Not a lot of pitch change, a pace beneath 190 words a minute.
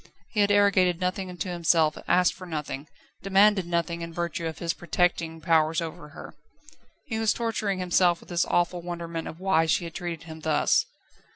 Yes: narrow, 2.1 semitones; average, 180 wpm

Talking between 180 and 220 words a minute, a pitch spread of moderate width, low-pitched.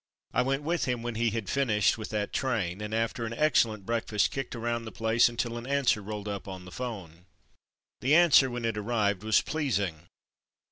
Yes: average, 195 wpm; average, 3.0 semitones; low, 115 Hz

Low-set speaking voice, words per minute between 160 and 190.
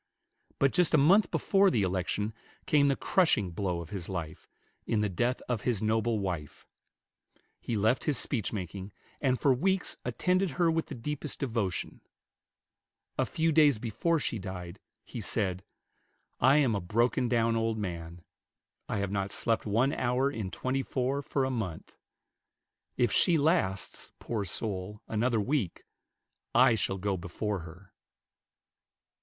No: low, 115 Hz; average, 150 wpm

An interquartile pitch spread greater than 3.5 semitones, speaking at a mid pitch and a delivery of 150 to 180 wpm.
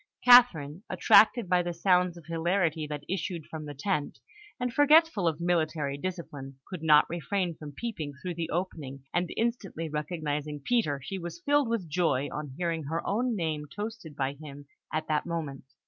Yes: average, 4.3 semitones; medium, 165 Hz; average, 170 wpm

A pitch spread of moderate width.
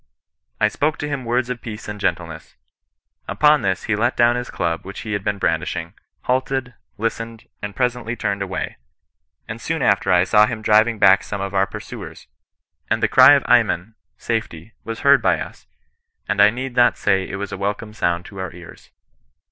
Yes: average, 3.6 semitones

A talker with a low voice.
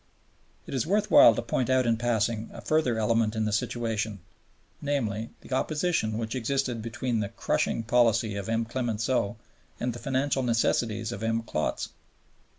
Yes: low, 115 Hz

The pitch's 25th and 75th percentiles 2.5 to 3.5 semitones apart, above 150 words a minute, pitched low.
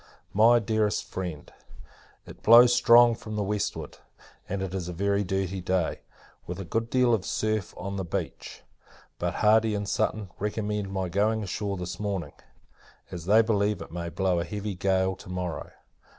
Yes: average, 2.8 semitones; average, 170 wpm; low, 100 Hz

